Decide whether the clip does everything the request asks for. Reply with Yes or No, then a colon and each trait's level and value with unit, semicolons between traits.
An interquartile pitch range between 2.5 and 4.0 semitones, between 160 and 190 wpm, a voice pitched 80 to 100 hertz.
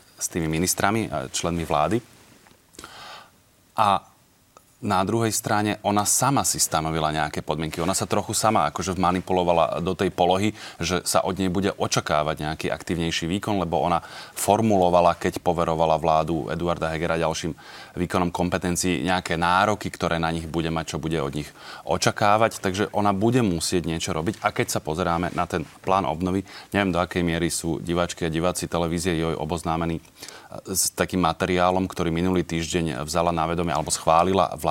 Yes: average, 2.8 semitones; fast, 165 wpm; very low, 90 Hz